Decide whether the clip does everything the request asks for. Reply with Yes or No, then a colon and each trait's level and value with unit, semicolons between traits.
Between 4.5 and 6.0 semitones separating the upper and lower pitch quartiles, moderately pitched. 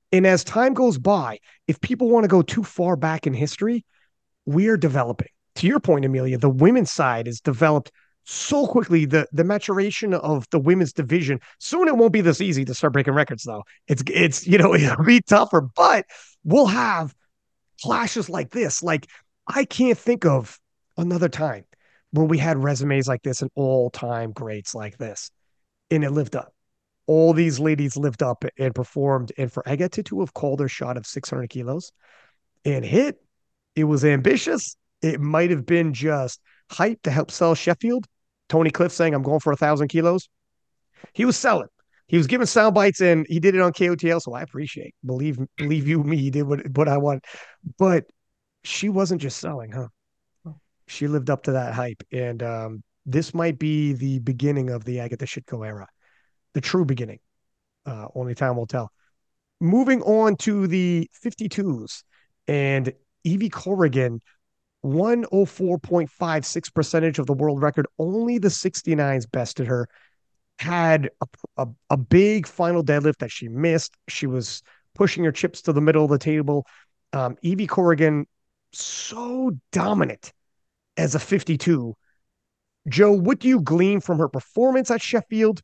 Yes: average, 5.2 semitones; medium, 155 Hz